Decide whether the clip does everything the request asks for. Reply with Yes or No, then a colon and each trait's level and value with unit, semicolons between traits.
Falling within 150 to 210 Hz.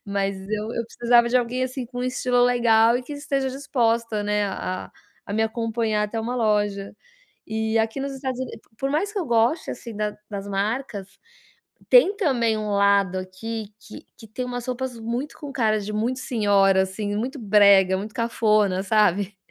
No: high, 225 Hz